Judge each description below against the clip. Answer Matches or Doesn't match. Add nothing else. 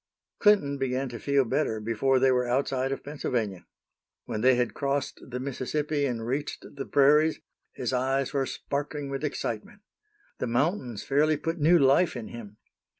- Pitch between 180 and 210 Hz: Doesn't match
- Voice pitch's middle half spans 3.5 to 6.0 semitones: Doesn't match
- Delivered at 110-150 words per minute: Doesn't match